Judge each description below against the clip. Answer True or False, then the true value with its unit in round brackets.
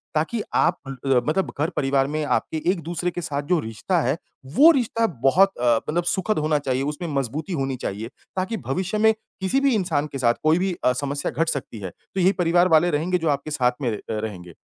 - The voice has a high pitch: False (155 Hz)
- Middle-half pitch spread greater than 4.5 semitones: True (5.2 semitones)